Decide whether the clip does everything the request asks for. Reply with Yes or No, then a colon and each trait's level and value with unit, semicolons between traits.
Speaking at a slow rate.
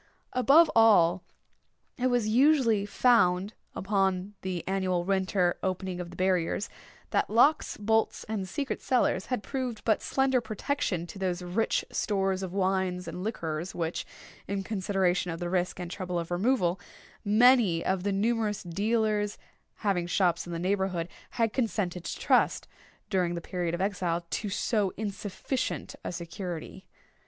No: average, 145 wpm